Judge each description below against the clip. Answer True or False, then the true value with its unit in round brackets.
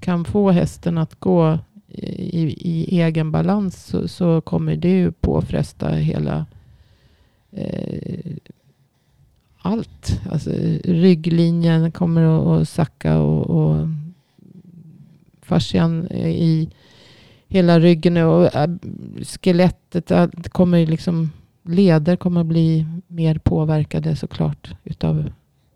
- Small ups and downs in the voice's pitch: True (1.8 semitones)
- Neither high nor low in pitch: True (165 Hz)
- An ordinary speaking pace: False (105 wpm)